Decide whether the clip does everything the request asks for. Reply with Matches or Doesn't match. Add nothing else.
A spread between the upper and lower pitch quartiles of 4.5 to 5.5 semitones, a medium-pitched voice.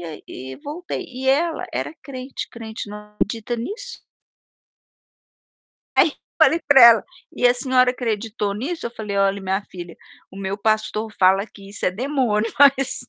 Doesn't match